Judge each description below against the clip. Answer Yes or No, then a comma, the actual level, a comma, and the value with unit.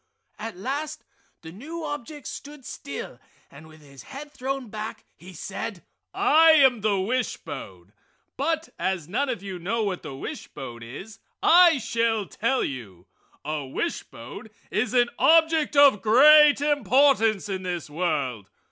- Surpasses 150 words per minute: No, average, 145 wpm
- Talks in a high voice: Yes, high, 220 Hz